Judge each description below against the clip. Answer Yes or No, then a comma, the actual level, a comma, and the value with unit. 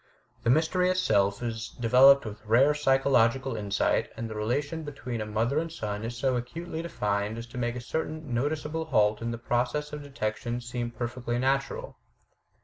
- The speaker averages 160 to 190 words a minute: Yes, average, 170 wpm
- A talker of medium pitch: No, low, 120 Hz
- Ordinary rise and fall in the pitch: Yes, average, 4.2 semitones